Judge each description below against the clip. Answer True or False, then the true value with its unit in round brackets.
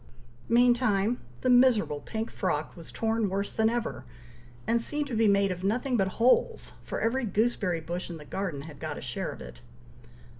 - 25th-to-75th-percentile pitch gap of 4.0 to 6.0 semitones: True (4.7 semitones)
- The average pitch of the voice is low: False (220 Hz)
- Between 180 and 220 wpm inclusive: True (185 wpm)